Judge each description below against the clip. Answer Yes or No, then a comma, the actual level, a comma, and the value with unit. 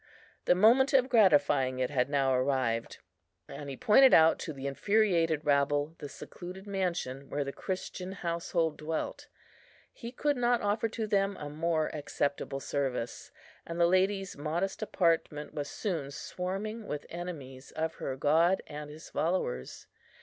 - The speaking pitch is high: No, medium, 160 Hz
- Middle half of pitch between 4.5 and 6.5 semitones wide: Yes, wide, 5.4 semitones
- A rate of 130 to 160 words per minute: Yes, average, 150 wpm